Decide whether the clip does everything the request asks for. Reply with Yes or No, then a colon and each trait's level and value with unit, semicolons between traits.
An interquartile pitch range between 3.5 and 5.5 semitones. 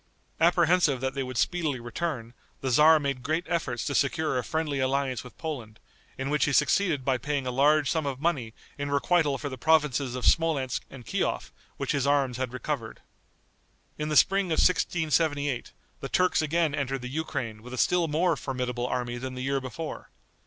Yes: average, 3.8 semitones